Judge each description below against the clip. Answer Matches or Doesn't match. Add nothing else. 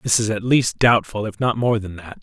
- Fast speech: Matches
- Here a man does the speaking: Matches